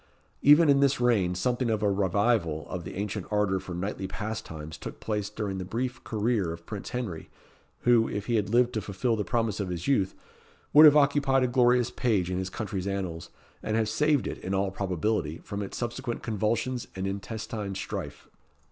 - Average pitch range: Yes, average, 4.2 semitones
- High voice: No, low, 105 Hz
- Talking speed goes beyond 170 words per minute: Yes, average, 190 wpm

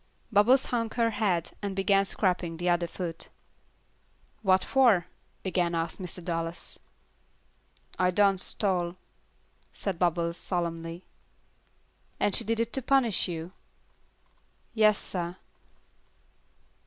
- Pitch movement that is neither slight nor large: Yes, average, 3.3 semitones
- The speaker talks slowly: Yes, slow, 110 wpm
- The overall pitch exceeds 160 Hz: Yes, medium, 185 Hz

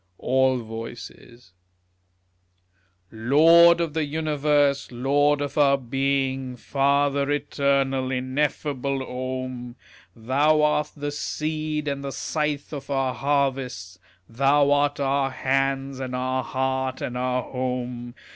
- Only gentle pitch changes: Yes, narrow, 2.0 semitones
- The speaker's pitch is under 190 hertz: Yes, low, 135 Hz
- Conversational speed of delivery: No, slow, 110 wpm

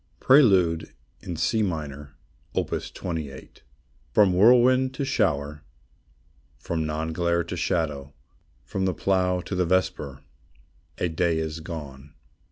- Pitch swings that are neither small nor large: Yes, average, 3.8 semitones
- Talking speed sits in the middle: No, slow, 120 wpm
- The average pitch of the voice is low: Yes, very low, 85 Hz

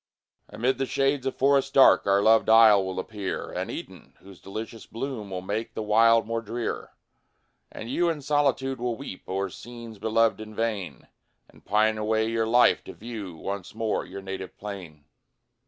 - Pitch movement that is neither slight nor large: Yes, average, 3.2 semitones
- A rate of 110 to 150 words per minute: No, average, 170 wpm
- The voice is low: Yes, low, 110 Hz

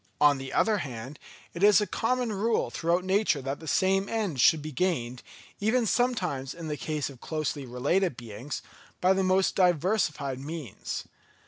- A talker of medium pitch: Yes, medium, 165 Hz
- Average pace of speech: Yes, average, 165 wpm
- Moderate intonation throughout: No, wide, 5.8 semitones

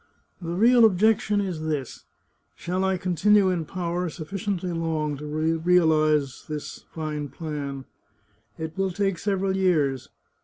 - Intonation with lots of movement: No, average, 3.7 semitones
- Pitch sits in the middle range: Yes, medium, 170 Hz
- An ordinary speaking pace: No, slow, 125 wpm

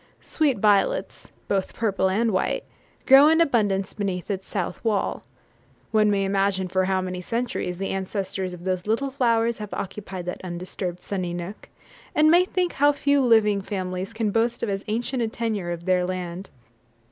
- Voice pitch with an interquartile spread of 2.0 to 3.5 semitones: No, average, 3.9 semitones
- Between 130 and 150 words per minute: No, average, 170 wpm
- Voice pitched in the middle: No, high, 200 Hz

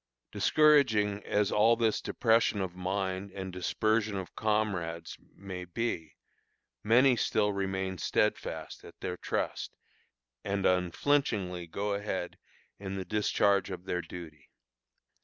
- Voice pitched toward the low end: Yes, low, 100 Hz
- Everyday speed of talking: No, slow, 120 wpm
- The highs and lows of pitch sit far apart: No, average, 2.9 semitones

